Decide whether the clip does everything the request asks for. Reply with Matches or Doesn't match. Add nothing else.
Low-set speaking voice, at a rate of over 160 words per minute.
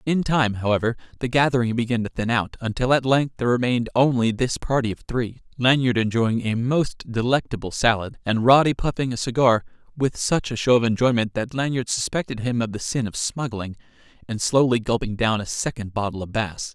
Matches